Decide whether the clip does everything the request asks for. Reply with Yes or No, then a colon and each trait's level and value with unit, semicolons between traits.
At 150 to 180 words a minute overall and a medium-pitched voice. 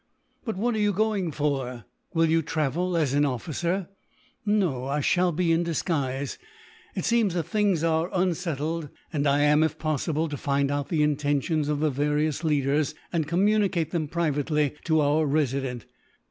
Yes: average, 165 wpm; medium, 155 Hz